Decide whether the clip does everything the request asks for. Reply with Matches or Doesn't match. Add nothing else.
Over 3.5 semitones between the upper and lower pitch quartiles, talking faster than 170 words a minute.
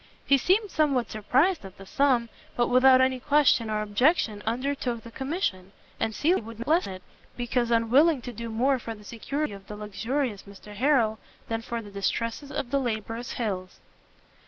Matches